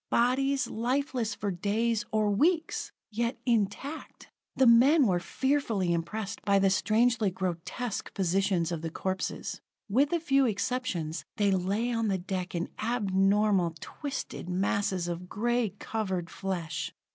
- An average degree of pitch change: Yes, average, 4.5 semitones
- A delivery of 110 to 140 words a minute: Yes, slow, 135 wpm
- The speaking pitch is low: No, high, 205 Hz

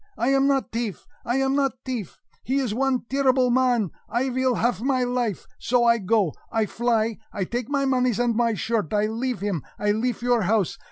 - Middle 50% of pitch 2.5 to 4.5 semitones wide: Yes, average, 2.9 semitones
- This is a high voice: Yes, high, 240 Hz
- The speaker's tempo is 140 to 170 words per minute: No, fast, 205 wpm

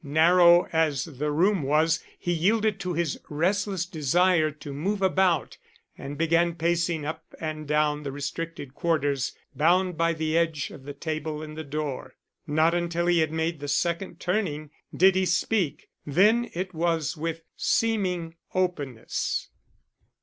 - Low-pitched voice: No, medium, 165 Hz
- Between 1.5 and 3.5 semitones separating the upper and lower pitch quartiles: Yes, average, 2.8 semitones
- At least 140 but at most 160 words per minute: Yes, average, 150 wpm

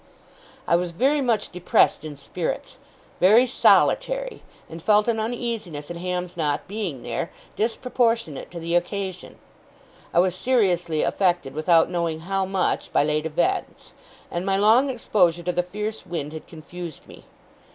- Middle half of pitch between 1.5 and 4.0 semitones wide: No, average, 4.5 semitones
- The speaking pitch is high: No, medium, 180 Hz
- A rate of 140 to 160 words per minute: Yes, average, 150 wpm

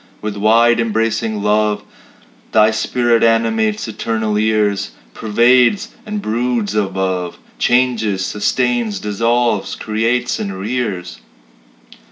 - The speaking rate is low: Yes, slow, 95 wpm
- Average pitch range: No, narrow, 2.2 semitones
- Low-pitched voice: Yes, low, 110 Hz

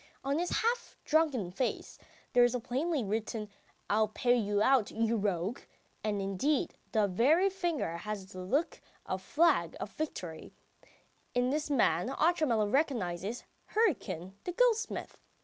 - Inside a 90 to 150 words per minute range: Yes, average, 140 wpm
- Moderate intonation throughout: No, wide, 7.2 semitones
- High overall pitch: Yes, high, 240 Hz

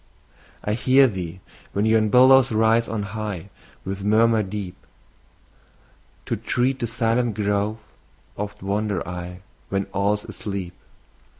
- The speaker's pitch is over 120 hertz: No, low, 105 Hz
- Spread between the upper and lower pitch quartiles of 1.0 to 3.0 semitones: Yes, narrow, 2.4 semitones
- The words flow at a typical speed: No, slow, 120 wpm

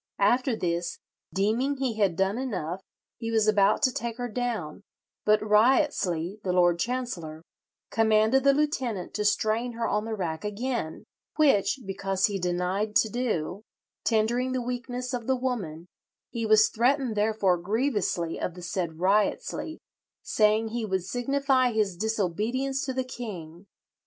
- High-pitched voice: Yes, high, 215 Hz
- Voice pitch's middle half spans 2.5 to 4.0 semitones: No, average, 4.6 semitones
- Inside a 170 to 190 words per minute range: No, average, 145 wpm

